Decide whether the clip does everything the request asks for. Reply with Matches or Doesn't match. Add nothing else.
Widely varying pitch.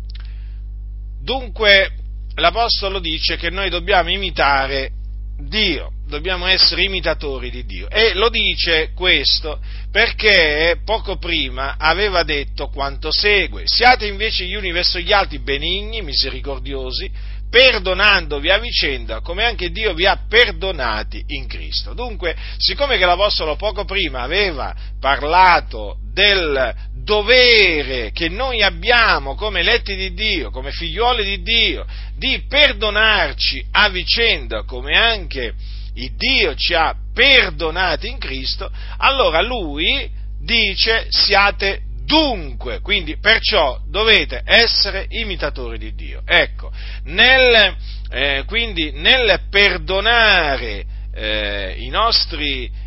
Matches